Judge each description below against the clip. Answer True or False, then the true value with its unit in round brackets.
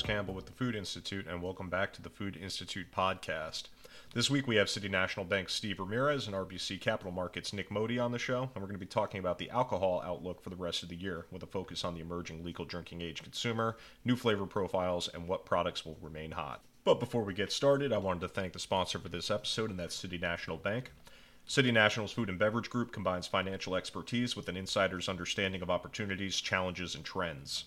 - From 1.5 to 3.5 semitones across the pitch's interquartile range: True (3.2 semitones)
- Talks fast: True (225 wpm)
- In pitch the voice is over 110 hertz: False (95 Hz)